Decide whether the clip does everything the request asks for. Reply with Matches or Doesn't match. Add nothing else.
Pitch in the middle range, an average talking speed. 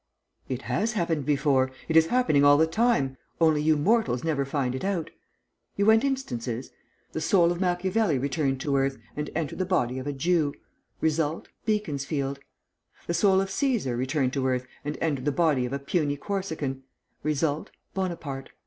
Matches